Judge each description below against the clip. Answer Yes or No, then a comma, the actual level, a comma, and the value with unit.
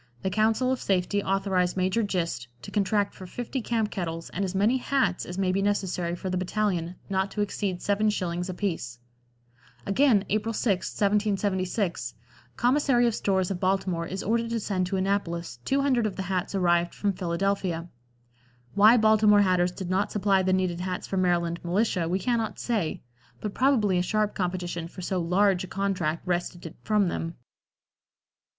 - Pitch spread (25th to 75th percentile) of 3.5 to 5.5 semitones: No, average, 2.8 semitones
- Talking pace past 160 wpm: Yes, average, 170 wpm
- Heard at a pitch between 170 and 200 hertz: Yes, high, 190 Hz